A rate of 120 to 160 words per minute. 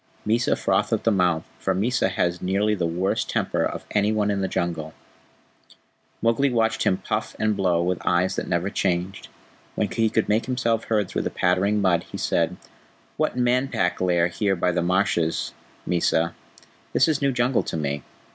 No: average, 185 wpm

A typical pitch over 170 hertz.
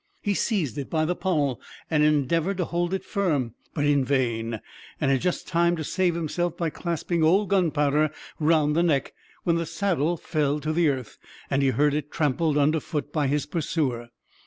No: medium, 155 Hz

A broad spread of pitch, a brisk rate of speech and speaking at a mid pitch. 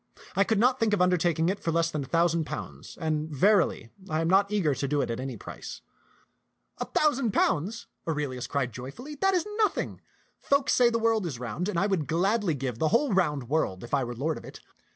Yes: wide, 6.7 semitones; fast, 225 wpm; medium, 165 Hz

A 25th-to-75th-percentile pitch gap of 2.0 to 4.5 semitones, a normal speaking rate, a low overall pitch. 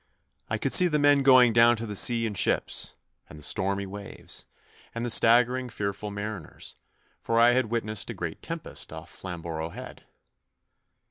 Yes: average, 3.4 semitones; average, 170 wpm; low, 115 Hz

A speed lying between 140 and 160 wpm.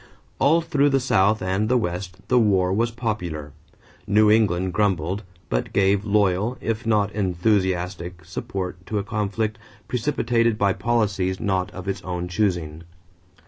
Yes: average, 145 wpm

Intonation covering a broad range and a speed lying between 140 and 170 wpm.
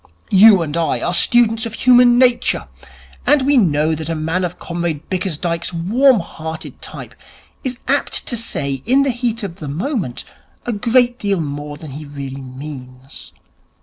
Yes: wide, 7.9 semitones; average, 165 wpm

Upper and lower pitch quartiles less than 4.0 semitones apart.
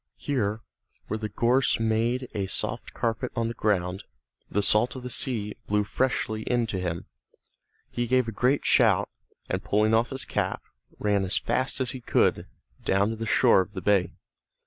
Yes: average, 3.1 semitones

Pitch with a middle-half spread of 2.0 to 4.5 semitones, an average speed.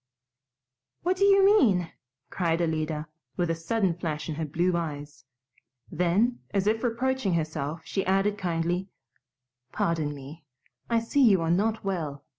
No: average, 5.2 semitones; average, 145 wpm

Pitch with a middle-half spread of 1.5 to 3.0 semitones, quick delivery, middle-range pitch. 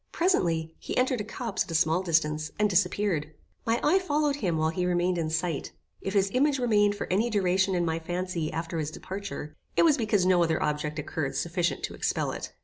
No: average, 4.5 semitones; fast, 210 wpm; medium, 180 Hz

